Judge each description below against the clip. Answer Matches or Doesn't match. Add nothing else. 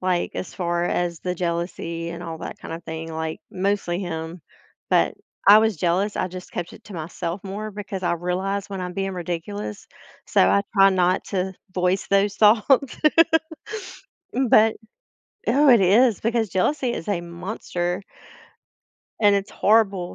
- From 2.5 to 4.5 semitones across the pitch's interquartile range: Matches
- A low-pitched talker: Doesn't match